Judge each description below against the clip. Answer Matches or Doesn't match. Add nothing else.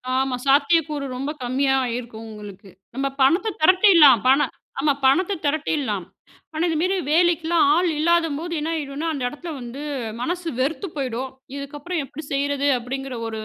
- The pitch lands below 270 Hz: Doesn't match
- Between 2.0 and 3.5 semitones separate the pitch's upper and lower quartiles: Doesn't match